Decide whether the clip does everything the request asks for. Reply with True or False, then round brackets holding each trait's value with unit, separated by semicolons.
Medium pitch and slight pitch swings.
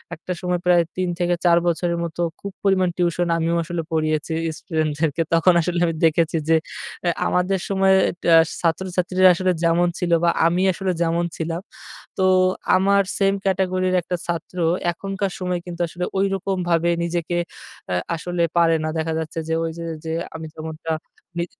True (175 Hz; 1.9 semitones)